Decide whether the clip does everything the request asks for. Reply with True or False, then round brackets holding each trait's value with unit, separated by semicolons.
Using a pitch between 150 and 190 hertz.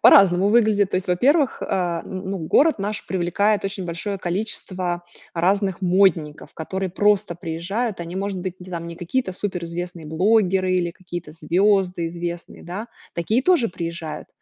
True (185 Hz)